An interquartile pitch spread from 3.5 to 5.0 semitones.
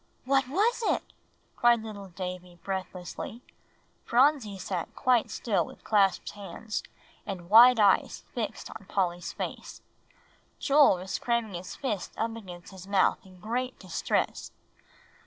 Yes: average, 4.4 semitones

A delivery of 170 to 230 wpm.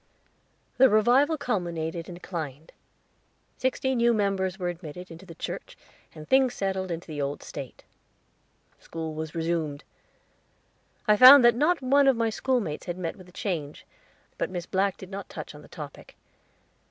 No: average, 160 wpm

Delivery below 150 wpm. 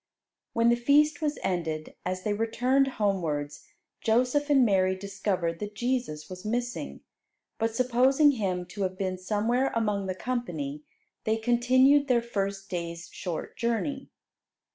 Yes: average, 140 wpm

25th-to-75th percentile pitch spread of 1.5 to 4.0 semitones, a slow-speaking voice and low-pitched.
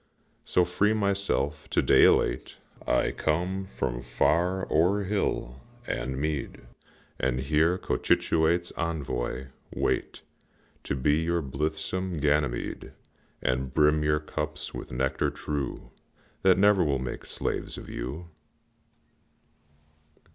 No: average, 4.9 semitones; slow, 110 wpm; very low, 75 Hz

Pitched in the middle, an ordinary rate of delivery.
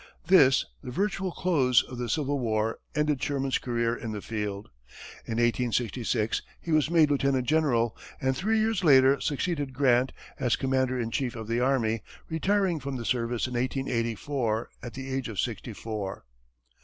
No: low, 130 Hz; average, 165 wpm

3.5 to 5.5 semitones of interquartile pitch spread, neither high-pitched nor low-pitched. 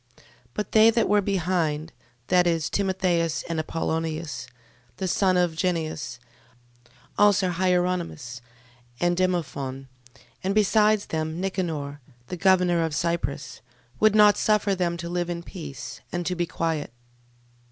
No: average, 2.8 semitones; medium, 175 Hz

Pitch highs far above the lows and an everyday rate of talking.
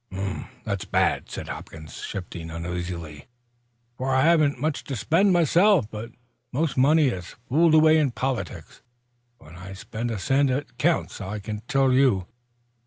Yes: wide, 8.2 semitones; average, 150 wpm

